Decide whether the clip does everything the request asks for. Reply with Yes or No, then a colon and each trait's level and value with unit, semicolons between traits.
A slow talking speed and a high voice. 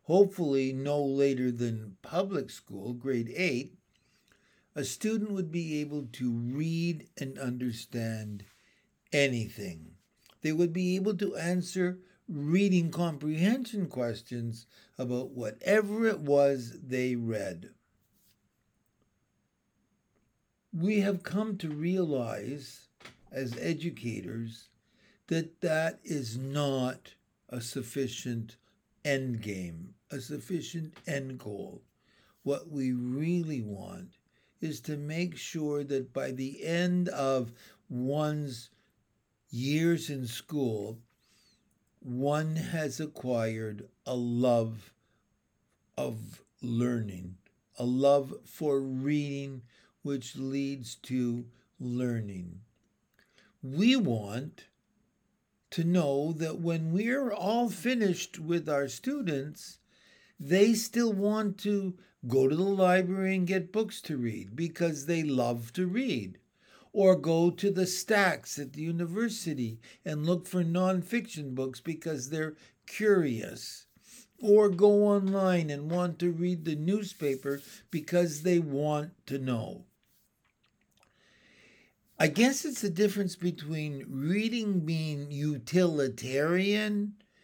No: slow, 105 wpm; medium, 150 Hz